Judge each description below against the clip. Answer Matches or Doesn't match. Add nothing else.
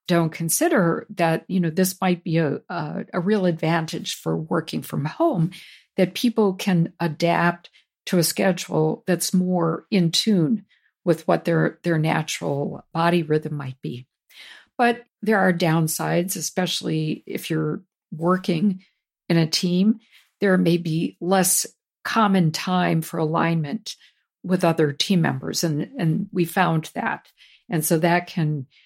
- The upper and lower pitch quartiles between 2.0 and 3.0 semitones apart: Matches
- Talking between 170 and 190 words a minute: Doesn't match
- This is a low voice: Doesn't match